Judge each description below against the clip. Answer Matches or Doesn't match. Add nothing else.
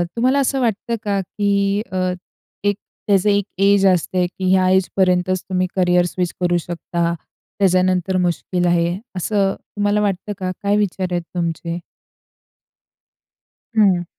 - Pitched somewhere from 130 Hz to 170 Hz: Doesn't match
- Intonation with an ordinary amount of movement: Doesn't match